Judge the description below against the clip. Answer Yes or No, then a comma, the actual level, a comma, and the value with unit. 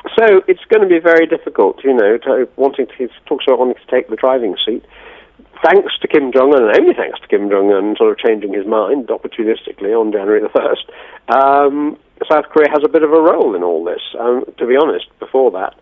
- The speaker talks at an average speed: No, fast, 230 wpm